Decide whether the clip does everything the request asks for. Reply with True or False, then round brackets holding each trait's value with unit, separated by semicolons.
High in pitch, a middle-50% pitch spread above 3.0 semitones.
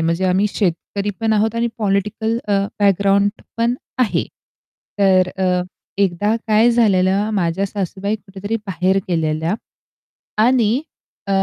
False (200 Hz; 2.7 semitones)